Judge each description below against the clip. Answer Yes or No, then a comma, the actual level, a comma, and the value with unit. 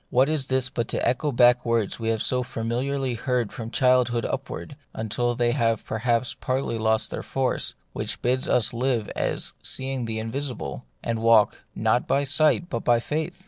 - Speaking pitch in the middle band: No, low, 120 Hz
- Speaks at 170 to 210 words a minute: Yes, average, 185 wpm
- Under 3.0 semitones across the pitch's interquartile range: Yes, narrow, 2.4 semitones